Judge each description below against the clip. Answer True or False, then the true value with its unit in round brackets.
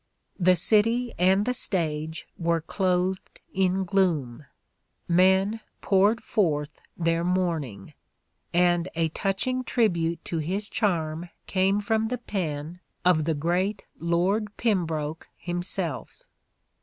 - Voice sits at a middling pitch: True (180 Hz)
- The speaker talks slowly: True (115 wpm)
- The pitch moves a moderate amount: True (3.2 semitones)